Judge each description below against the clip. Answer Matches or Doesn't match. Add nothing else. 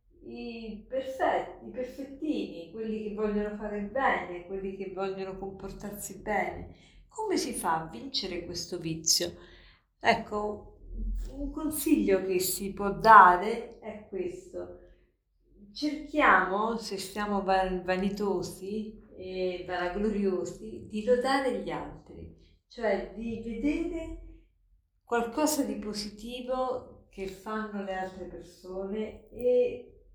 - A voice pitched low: Doesn't match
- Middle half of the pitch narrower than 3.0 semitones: Doesn't match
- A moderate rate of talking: Doesn't match